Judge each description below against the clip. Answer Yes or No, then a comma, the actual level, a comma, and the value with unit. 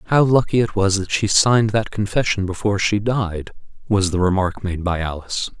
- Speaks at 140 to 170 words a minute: No, average, 195 wpm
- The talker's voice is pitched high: No, low, 100 Hz